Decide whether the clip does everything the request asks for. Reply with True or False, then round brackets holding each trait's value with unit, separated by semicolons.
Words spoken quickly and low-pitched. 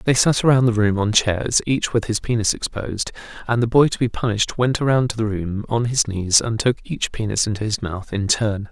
True (235 wpm; 110 Hz)